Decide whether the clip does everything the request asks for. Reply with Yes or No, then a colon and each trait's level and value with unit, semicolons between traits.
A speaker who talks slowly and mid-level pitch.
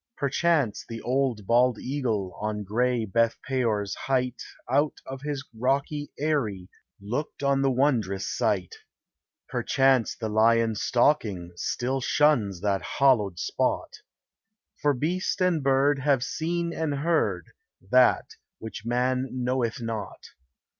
No: slow, 120 wpm; low, 125 Hz